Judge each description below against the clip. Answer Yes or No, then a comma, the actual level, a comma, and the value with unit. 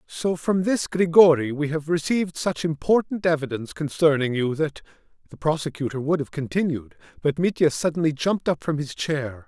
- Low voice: No, medium, 155 Hz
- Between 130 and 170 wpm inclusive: Yes, average, 165 wpm